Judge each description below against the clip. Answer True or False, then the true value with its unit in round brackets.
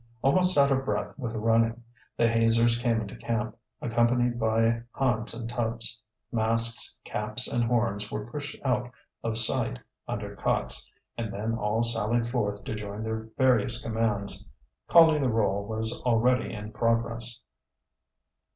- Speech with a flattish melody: True (1.5 semitones)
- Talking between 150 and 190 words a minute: False (140 wpm)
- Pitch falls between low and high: False (115 Hz)